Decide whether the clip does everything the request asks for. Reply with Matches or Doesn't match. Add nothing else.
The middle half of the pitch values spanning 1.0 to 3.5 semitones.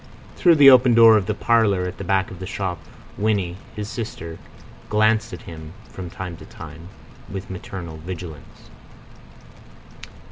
Doesn't match